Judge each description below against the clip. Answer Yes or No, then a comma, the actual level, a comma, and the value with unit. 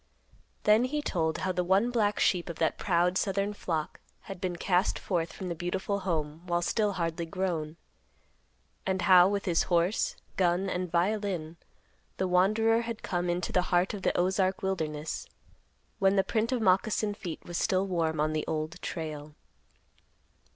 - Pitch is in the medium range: Yes, medium, 180 Hz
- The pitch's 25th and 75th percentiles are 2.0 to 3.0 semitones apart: Yes, average, 2.7 semitones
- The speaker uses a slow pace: No, average, 165 wpm